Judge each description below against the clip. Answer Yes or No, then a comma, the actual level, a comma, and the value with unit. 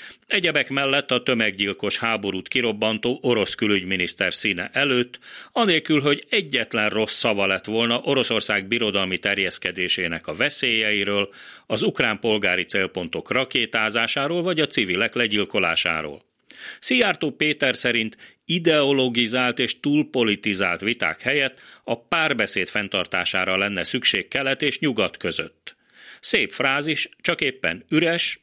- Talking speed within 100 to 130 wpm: Yes, average, 110 wpm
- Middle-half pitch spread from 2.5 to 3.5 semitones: No, average, 5.1 semitones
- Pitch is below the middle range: Yes, low, 115 Hz